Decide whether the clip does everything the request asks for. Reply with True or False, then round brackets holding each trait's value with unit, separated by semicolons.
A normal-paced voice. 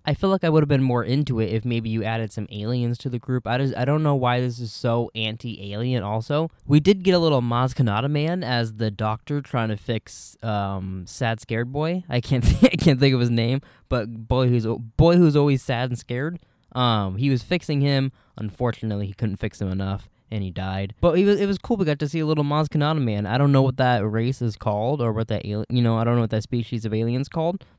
False (255 wpm)